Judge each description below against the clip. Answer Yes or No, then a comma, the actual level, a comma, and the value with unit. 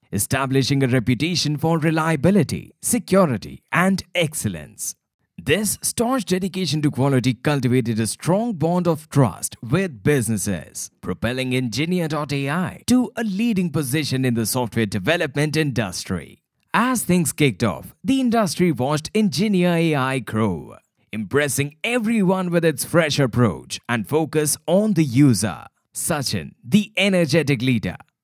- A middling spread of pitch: No, wide, 6.1 semitones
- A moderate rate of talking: No, slow, 120 wpm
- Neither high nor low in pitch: Yes, medium, 150 Hz